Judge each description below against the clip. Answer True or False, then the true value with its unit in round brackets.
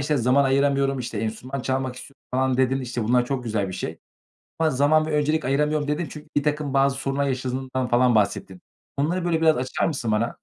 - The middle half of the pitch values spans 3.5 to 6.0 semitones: False (2.7 semitones)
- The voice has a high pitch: False (135 Hz)